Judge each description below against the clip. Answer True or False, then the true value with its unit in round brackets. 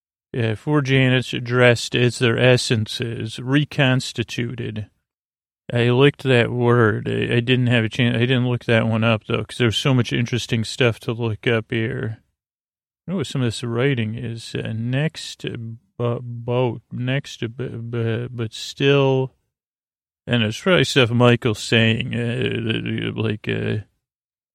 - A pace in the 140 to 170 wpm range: True (145 wpm)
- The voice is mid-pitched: False (120 Hz)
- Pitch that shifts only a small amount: True (1.9 semitones)